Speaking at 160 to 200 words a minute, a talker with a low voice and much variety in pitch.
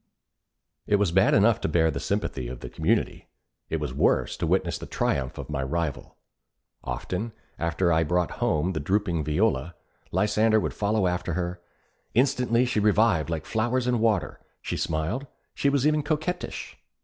Yes: average, 170 wpm; very low, 95 Hz; wide, 5.9 semitones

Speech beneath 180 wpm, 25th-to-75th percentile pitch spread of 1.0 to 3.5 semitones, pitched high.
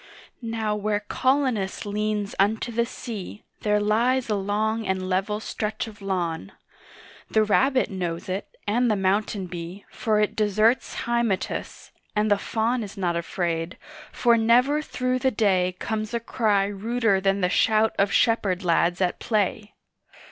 Yes: average, 150 wpm; average, 2.8 semitones; high, 210 Hz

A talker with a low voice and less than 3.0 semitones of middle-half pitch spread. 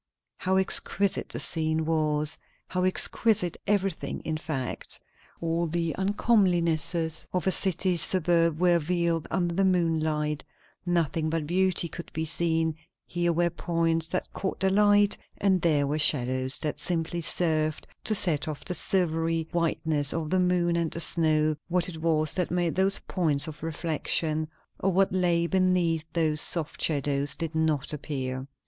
No: medium, 165 Hz; narrow, 2.5 semitones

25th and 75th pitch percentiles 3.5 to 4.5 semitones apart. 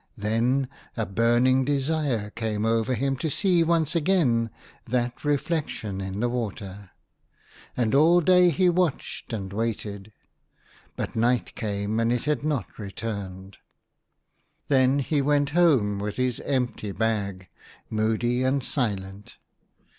No: average, 5.2 semitones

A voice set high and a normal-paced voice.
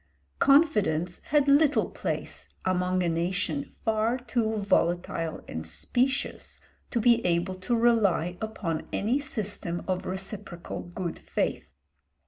No: high, 200 Hz; slow, 115 wpm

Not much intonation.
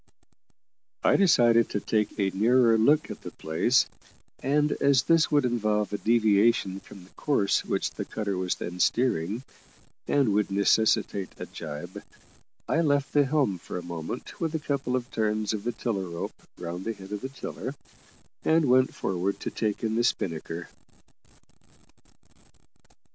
No: average, 5.0 semitones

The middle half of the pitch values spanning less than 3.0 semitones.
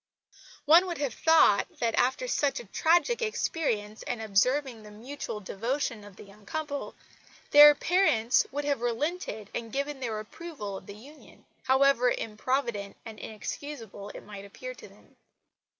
No: wide, 5.6 semitones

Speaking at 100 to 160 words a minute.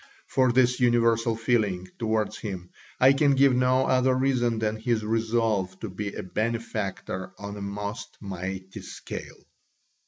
Yes: average, 145 wpm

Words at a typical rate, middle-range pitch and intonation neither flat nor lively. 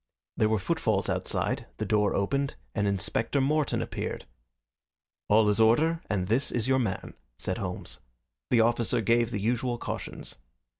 No: average, 155 wpm; low, 115 Hz; average, 3.9 semitones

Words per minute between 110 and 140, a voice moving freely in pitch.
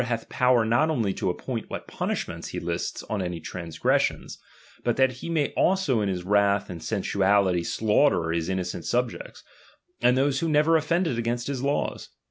No: average, 175 wpm; wide, 6.6 semitones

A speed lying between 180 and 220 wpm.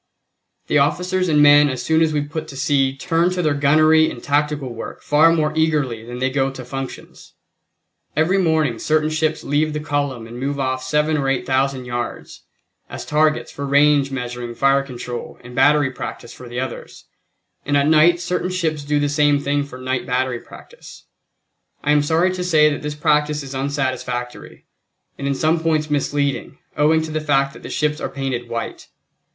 Yes: average, 190 wpm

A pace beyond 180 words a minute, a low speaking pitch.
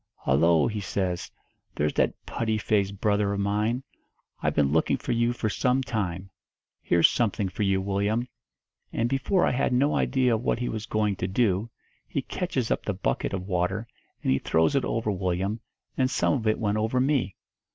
Yes: average, 190 wpm; low, 105 Hz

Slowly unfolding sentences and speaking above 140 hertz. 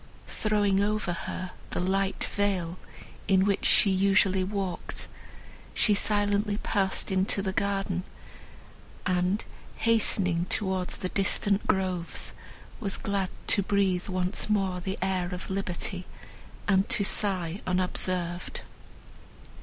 Yes: slow, 115 wpm; high, 190 Hz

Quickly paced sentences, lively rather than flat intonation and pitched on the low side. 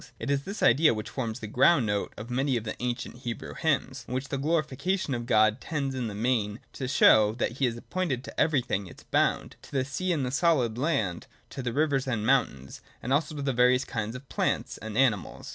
No: fast, 230 wpm; average, 3.7 semitones; low, 130 Hz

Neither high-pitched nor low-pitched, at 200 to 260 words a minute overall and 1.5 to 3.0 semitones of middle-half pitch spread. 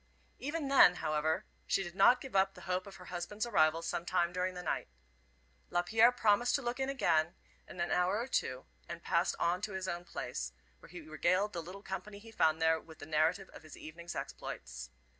No: medium, 180 Hz; fast, 205 wpm; average, 4.2 semitones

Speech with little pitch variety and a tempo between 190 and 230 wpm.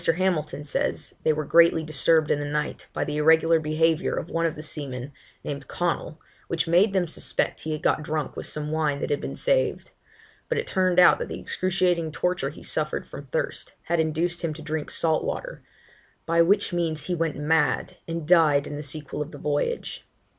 Yes: narrow, 2.3 semitones; average, 200 wpm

